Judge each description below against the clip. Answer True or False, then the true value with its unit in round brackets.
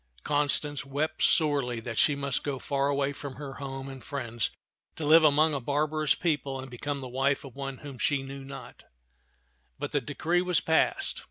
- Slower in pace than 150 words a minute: False (185 wpm)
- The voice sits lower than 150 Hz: True (140 Hz)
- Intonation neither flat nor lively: False (1.7 semitones)